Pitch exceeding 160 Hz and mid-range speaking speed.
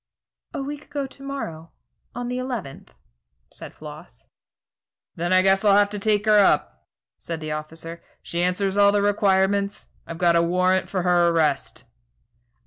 Yes: high, 190 Hz; average, 160 wpm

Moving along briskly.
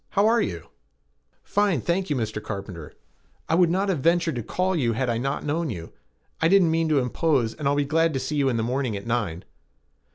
Yes: fast, 225 wpm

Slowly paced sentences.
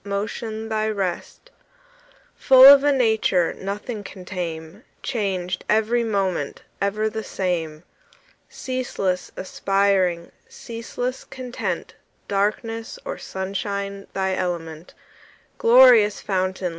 Yes: slow, 95 wpm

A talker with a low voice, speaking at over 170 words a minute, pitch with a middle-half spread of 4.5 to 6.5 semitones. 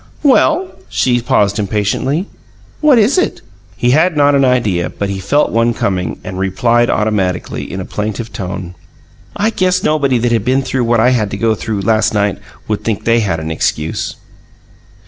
Yes: low, 115 Hz; average, 180 wpm; average, 5.2 semitones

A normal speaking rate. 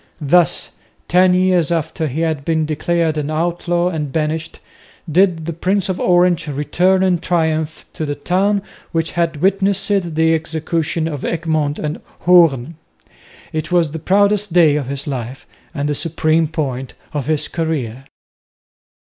Yes: average, 150 wpm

